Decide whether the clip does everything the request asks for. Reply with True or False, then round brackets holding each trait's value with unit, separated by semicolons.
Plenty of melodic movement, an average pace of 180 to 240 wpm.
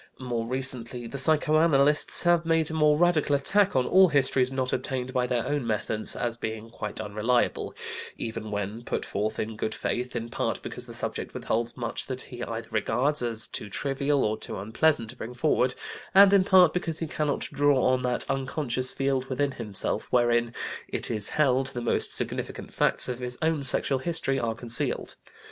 False (3.9 semitones; 185 wpm)